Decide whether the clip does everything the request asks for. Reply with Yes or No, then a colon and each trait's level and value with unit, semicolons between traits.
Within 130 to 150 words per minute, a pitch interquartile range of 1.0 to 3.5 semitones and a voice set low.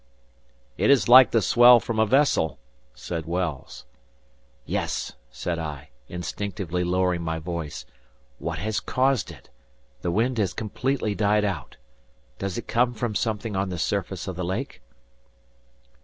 No: average, 140 wpm; average, 4.8 semitones; low, 100 Hz